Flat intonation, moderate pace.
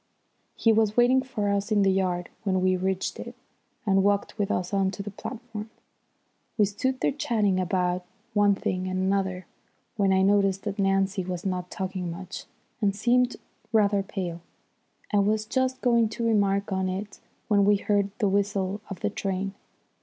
Yes: narrow, 2.0 semitones; average, 175 wpm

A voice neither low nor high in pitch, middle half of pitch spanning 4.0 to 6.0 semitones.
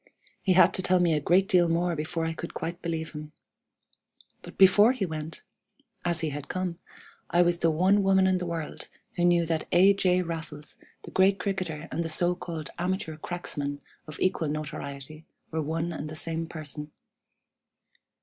No: medium, 170 Hz; average, 2.7 semitones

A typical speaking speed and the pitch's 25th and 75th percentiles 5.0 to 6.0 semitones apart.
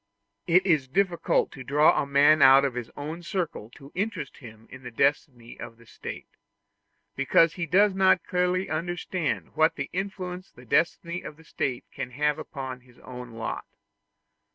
Yes: average, 165 wpm; wide, 5.5 semitones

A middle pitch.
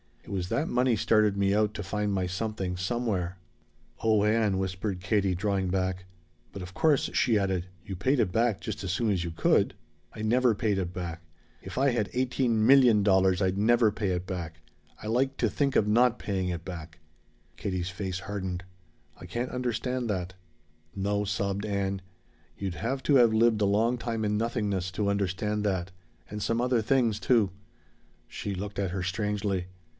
No: low, 100 Hz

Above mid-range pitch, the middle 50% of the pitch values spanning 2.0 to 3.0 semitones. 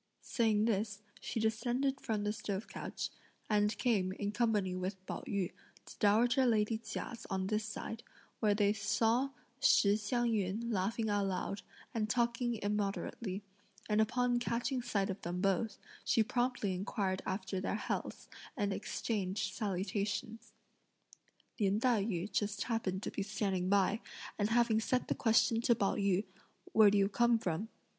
Yes: high, 210 Hz; narrow, 2.5 semitones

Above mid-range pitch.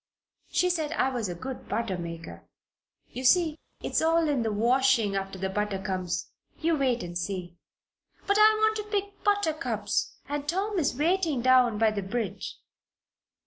Yes: very high, 255 Hz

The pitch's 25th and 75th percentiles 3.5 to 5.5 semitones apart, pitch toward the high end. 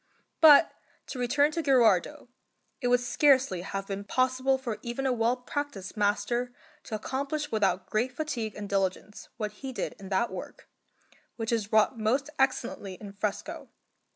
Yes: average, 4.4 semitones; high, 235 Hz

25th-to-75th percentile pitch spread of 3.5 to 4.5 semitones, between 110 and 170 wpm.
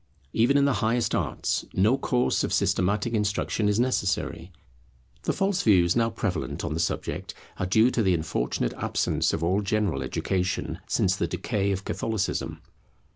Yes: average, 4.2 semitones; average, 160 wpm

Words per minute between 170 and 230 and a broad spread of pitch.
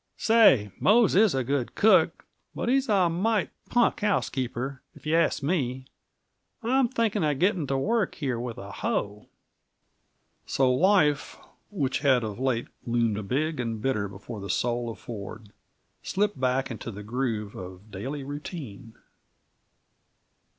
No: average, 145 wpm; wide, 7.9 semitones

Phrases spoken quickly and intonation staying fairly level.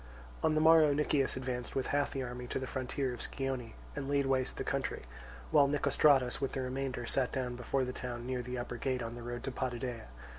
Yes: fast, 220 wpm; narrow, 1.8 semitones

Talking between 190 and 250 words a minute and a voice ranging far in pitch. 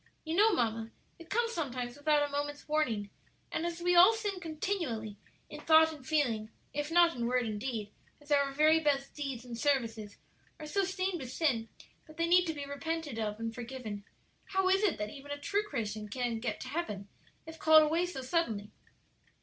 Yes: average, 200 wpm; wide, 6.1 semitones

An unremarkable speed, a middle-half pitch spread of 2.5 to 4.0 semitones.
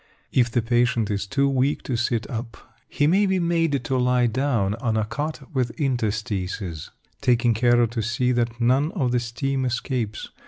Yes: average, 180 wpm; average, 2.9 semitones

